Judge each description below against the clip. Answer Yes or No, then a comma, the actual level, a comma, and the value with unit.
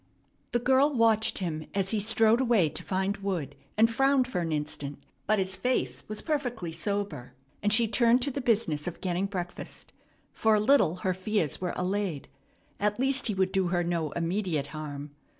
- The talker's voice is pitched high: Yes, high, 195 Hz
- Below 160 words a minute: No, average, 185 wpm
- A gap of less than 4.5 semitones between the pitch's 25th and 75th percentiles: No, average, 5.1 semitones